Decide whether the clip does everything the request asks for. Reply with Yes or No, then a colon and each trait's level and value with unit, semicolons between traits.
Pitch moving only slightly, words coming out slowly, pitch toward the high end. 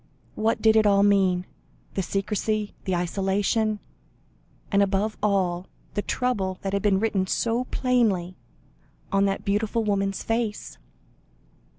Yes: narrow, 2.1 semitones; slow, 125 wpm; high, 200 Hz